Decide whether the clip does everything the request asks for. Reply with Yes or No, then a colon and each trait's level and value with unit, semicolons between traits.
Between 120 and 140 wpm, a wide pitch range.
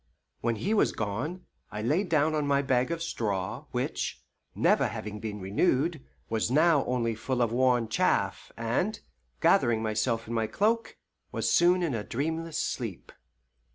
No: average, 155 wpm; wide, 6.2 semitones